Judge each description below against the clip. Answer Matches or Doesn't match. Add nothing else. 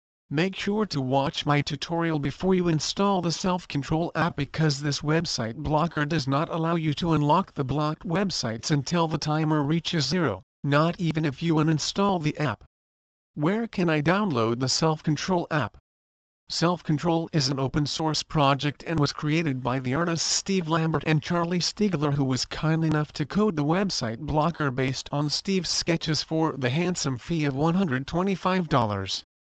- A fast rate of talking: Doesn't match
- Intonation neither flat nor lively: Matches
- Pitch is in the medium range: Matches